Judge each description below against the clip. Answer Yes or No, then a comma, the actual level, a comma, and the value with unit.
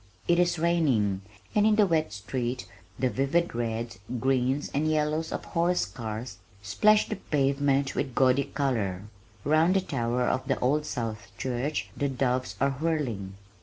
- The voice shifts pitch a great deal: No, average, 4.7 semitones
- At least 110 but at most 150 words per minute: No, average, 160 wpm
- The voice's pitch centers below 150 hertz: Yes, low, 135 Hz